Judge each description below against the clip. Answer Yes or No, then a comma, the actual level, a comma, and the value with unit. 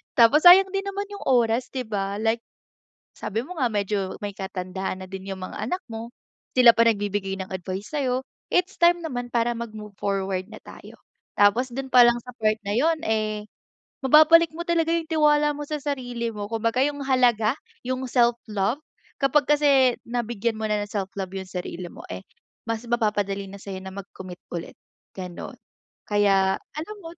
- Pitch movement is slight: No, average, 5.3 semitones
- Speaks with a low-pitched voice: No, high, 230 Hz